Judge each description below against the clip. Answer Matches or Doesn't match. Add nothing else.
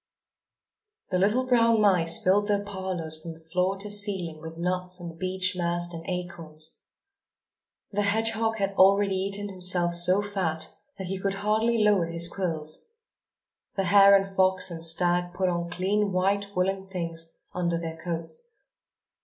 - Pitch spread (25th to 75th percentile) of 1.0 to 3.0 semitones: Matches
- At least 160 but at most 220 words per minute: Doesn't match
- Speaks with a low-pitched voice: Doesn't match